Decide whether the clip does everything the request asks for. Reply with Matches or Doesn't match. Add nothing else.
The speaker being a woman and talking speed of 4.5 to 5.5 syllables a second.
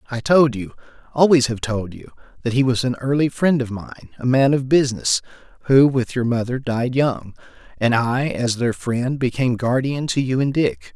Doesn't match